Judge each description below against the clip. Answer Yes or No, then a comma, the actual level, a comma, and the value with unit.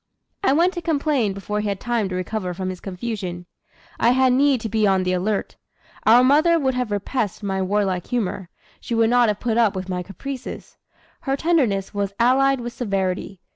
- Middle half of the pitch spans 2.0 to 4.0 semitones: No, average, 5.0 semitones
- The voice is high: Yes, high, 215 Hz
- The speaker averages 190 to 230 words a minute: Yes, average, 195 wpm